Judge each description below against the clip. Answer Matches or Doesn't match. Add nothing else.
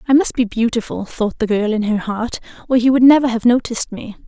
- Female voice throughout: Matches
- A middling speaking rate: Doesn't match